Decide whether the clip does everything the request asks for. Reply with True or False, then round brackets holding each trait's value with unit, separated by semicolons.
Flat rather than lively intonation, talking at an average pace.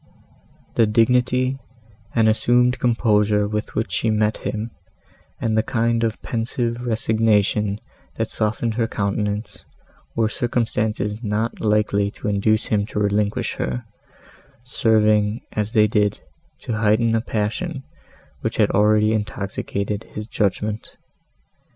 False (1.7 semitones; 120 wpm)